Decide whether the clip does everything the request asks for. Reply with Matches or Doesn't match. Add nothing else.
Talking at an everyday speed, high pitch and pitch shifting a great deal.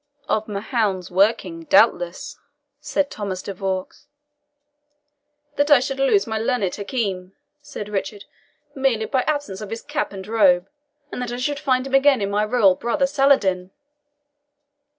Matches